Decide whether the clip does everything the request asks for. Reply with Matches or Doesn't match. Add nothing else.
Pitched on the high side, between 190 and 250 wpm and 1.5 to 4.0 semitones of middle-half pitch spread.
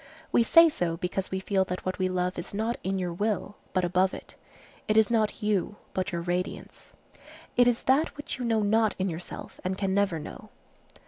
Matches